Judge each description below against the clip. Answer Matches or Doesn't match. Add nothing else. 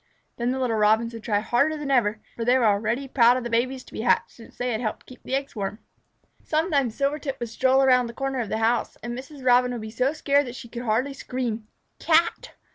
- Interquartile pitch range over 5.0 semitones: Doesn't match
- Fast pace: Matches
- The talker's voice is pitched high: Matches